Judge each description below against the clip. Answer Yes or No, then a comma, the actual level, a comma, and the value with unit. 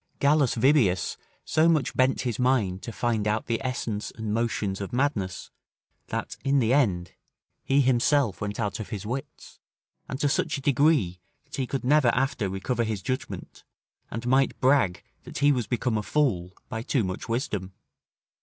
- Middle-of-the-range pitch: No, low, 120 Hz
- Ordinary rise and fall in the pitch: Yes, average, 4.7 semitones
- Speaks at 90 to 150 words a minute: No, average, 175 wpm